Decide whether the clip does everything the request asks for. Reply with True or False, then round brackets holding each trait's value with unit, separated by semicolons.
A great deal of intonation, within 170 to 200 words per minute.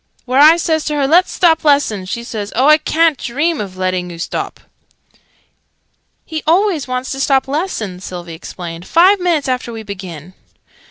True (8.8 semitones; 175 wpm)